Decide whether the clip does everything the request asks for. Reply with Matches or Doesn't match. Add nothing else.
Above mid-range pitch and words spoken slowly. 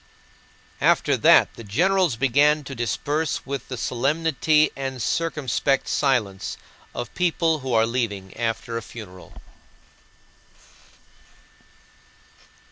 Doesn't match